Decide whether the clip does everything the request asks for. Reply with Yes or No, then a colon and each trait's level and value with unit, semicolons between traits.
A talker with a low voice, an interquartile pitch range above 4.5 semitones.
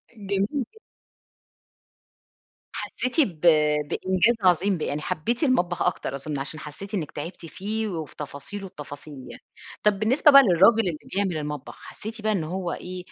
No: medium, 185 Hz; wide, 5.6 semitones